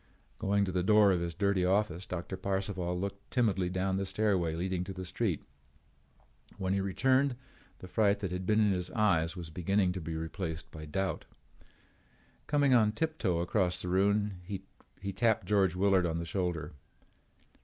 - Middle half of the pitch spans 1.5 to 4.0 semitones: Yes, narrow, 2.4 semitones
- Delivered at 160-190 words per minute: Yes, average, 170 wpm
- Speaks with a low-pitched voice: Yes, very low, 95 Hz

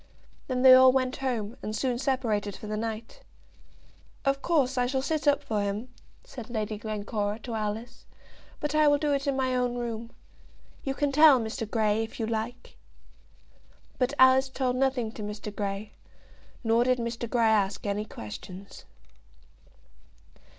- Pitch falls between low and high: No, high, 240 Hz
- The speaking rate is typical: Yes, average, 160 wpm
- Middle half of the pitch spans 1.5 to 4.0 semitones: Yes, average, 3.6 semitones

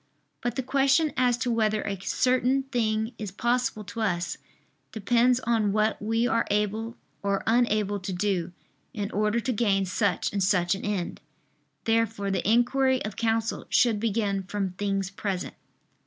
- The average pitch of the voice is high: Yes, high, 215 Hz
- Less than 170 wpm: Yes, average, 155 wpm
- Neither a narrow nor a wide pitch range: Yes, average, 3.1 semitones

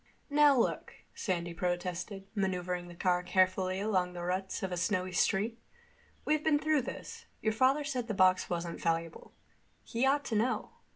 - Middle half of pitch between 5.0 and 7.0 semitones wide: Yes, wide, 5.5 semitones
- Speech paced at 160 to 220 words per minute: Yes, average, 165 wpm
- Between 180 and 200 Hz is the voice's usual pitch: Yes, high, 190 Hz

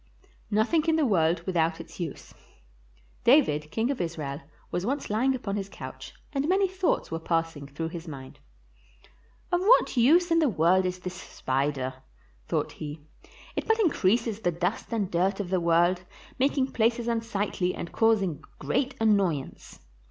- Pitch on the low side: No, high, 190 Hz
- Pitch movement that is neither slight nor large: No, wide, 6.9 semitones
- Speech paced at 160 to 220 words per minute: Yes, average, 165 wpm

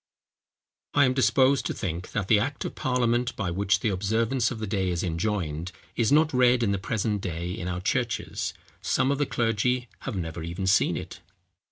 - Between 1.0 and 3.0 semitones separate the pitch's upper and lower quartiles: No, average, 5.3 semitones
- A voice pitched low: Yes, low, 105 Hz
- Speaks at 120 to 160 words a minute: No, average, 200 wpm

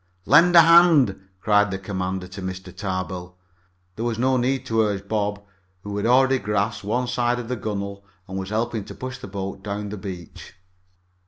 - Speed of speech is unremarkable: Yes, average, 185 wpm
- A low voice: Yes, low, 105 Hz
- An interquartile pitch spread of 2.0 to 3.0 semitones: No, average, 4.0 semitones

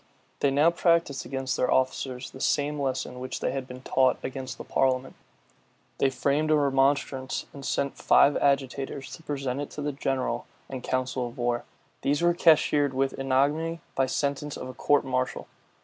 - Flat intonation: Yes, narrow, 1.8 semitones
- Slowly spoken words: No, average, 175 wpm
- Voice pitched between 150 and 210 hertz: No, low, 135 Hz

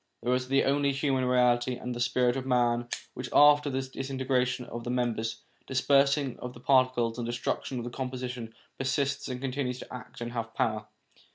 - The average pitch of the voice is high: No, low, 125 Hz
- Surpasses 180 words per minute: Yes, average, 200 wpm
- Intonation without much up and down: Yes, narrow, 1.8 semitones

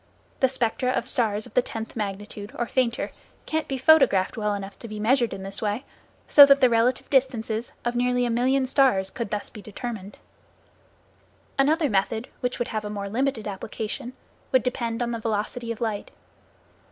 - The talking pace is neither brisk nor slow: Yes, average, 180 wpm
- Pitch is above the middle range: Yes, high, 230 Hz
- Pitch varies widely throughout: No, average, 3.3 semitones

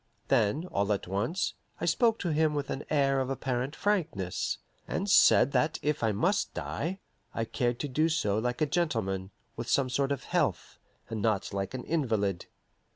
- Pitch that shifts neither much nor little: No, wide, 6.2 semitones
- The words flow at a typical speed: Yes, average, 180 wpm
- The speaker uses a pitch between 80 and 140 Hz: Yes, low, 135 Hz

